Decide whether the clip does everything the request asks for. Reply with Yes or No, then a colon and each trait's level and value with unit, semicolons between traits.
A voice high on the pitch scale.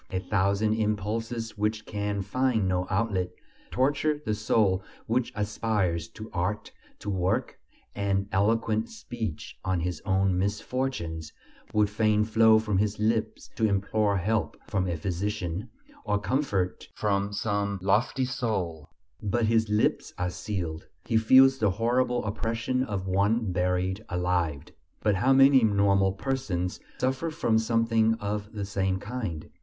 No: low, 105 Hz